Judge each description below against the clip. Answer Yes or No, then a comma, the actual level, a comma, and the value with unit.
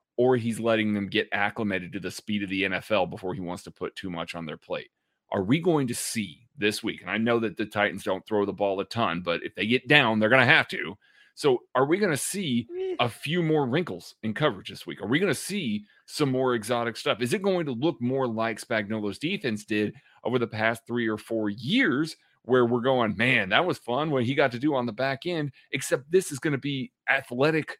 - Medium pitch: No, low, 120 Hz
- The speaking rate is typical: No, fast, 245 wpm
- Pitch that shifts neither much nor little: No, wide, 5.7 semitones